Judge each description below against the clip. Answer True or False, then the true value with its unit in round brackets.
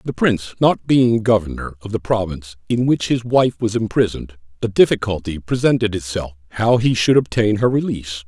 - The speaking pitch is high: False (110 Hz)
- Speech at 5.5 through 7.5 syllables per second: True (5.6 syllables/s)